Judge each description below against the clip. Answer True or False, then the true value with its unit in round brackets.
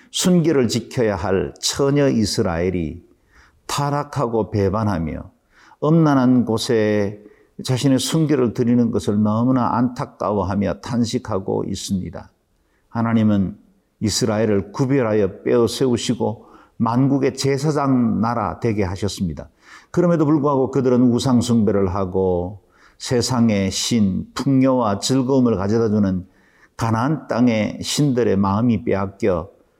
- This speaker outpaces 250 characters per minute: True (275 characters per minute)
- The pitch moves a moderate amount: True (4.6 semitones)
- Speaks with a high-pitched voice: False (115 Hz)